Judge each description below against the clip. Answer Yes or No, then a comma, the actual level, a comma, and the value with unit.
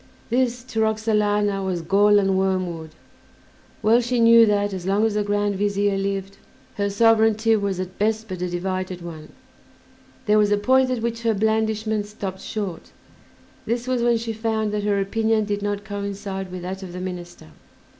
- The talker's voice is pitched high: Yes, high, 205 Hz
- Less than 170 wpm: No, average, 175 wpm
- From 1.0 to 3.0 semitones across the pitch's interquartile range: Yes, narrow, 2.4 semitones